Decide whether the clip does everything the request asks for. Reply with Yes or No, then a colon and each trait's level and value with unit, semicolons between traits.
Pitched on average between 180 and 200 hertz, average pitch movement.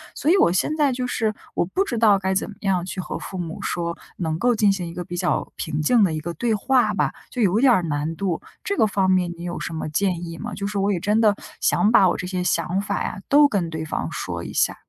Yes: high, 190 Hz; average, 4.0 semitones